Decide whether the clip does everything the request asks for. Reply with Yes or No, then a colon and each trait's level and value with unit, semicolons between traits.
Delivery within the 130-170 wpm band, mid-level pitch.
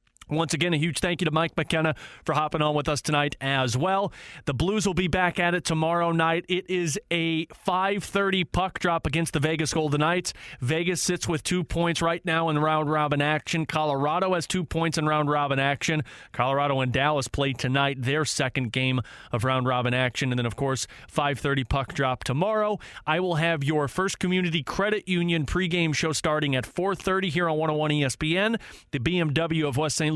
No: average, 195 wpm; medium, 160 Hz